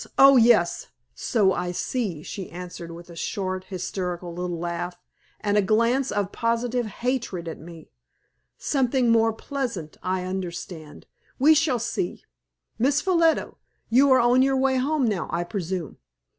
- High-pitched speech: Yes, high, 205 Hz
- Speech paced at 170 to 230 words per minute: No, average, 145 wpm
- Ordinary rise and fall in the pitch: No, wide, 6.2 semitones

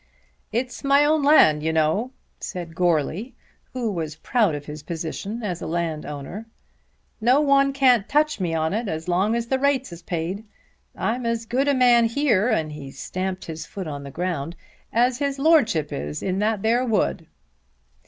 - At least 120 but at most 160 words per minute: No, average, 175 wpm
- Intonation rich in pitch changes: Yes, wide, 7.5 semitones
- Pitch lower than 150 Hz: No, high, 205 Hz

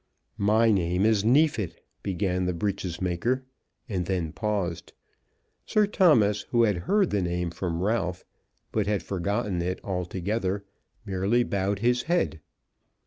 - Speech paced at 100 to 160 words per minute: Yes, slow, 135 wpm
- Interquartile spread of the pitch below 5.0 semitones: Yes, average, 3.8 semitones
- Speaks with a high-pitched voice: No, low, 100 Hz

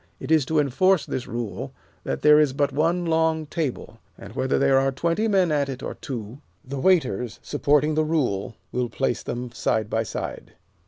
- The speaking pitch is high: No, medium, 140 Hz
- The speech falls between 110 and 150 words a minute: No, average, 190 wpm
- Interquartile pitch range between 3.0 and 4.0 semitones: No, average, 4.4 semitones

